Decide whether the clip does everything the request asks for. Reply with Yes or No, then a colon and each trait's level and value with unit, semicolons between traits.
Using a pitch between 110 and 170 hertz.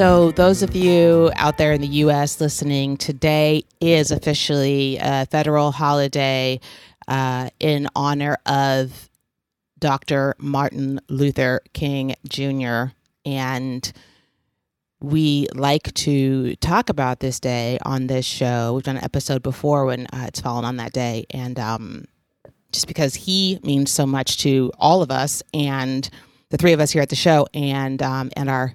Yes: medium, 140 Hz